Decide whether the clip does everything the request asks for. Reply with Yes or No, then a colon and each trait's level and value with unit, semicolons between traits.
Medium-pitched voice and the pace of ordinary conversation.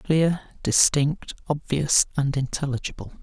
No: medium, 145 Hz; slow, 95 wpm